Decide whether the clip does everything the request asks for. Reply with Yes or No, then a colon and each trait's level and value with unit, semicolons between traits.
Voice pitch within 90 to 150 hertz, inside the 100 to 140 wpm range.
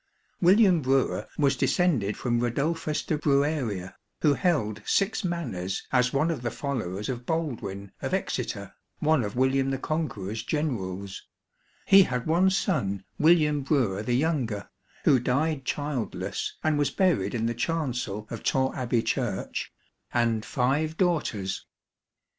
Yes: low, 135 Hz; slow, 135 wpm